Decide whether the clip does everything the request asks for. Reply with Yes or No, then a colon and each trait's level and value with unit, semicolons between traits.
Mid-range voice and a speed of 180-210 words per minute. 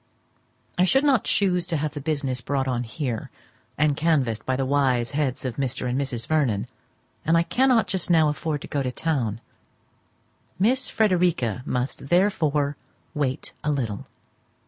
No: medium, 145 Hz; average, 160 wpm